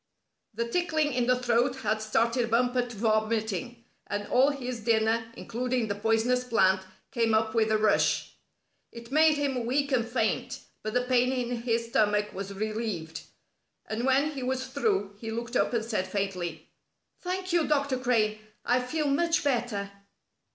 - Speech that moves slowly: No, average, 165 wpm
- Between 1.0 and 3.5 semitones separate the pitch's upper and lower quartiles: Yes, average, 2.9 semitones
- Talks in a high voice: Yes, high, 235 Hz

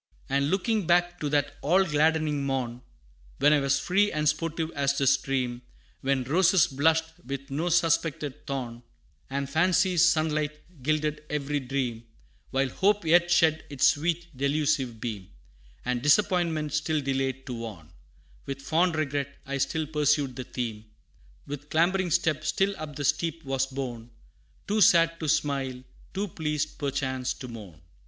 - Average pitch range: Yes, average, 3.3 semitones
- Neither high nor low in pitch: Yes, medium, 150 Hz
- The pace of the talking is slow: No, average, 150 wpm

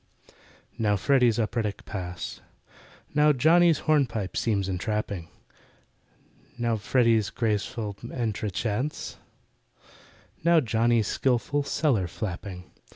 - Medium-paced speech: No, slow, 85 wpm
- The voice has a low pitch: Yes, low, 115 Hz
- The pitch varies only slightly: No, average, 4.2 semitones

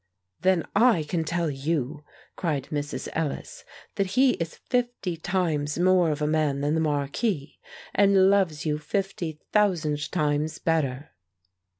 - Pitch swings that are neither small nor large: Yes, average, 4.1 semitones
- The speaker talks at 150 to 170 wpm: No, slow, 135 wpm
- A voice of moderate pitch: Yes, medium, 160 Hz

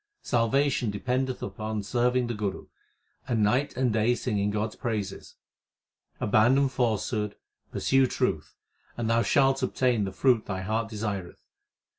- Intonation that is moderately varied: Yes, average, 3.3 semitones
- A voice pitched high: No, low, 115 Hz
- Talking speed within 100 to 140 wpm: Yes, slow, 135 wpm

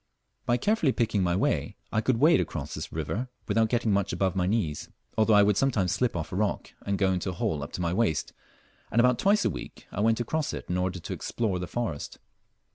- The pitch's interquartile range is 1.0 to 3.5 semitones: No, average, 4.7 semitones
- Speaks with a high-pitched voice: No, low, 100 Hz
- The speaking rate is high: Yes, fast, 230 wpm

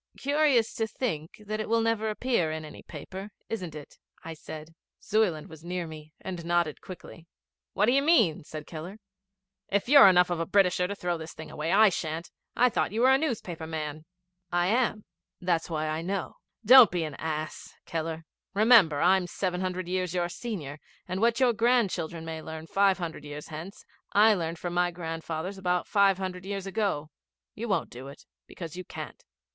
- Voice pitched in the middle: Yes, medium, 180 Hz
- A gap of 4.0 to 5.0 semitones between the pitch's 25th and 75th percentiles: Yes, average, 4.6 semitones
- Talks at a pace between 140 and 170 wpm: No, average, 190 wpm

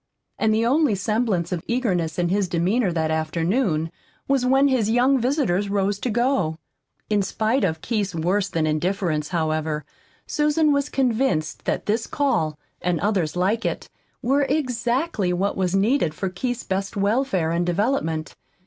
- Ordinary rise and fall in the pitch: No, wide, 6.4 semitones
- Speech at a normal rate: Yes, average, 155 wpm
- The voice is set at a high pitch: Yes, high, 200 Hz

